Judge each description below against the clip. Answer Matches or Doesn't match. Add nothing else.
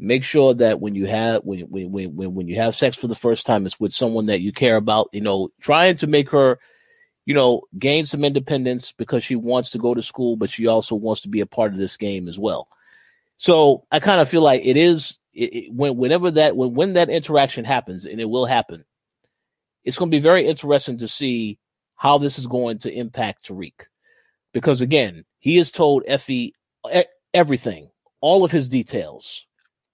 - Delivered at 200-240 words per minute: Matches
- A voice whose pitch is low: Matches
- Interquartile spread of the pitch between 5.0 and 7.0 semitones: Matches